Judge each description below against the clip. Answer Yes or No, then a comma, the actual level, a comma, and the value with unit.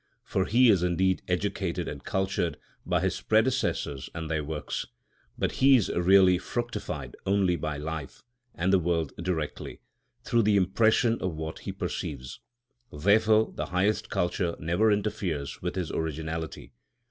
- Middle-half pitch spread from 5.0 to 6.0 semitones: No, average, 4.3 semitones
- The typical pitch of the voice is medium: No, very low, 90 Hz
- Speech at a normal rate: Yes, average, 145 wpm